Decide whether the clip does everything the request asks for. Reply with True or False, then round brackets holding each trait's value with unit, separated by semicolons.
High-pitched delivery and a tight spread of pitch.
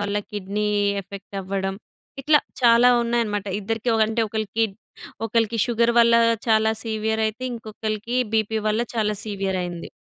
True (220 Hz; 2.0 semitones)